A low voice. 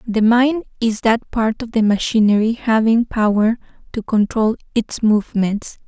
No: high, 220 Hz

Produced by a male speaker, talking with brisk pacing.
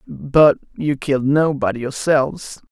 No: male; slow, 110 wpm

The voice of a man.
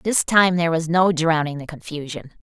No: female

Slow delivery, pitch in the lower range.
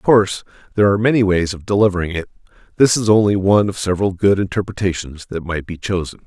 No: average, 200 wpm; very low, 95 Hz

